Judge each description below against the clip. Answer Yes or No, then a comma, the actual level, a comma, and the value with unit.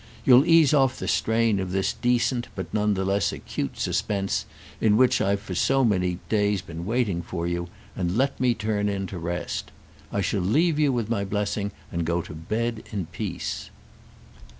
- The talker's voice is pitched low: Yes, low, 105 Hz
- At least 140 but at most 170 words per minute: No, average, 185 wpm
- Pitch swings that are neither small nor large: Yes, average, 4.6 semitones